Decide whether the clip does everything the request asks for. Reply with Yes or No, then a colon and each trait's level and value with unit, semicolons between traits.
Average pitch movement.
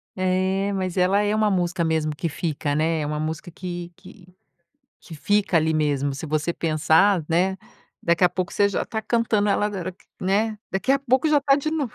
Yes: average, 4.3 semitones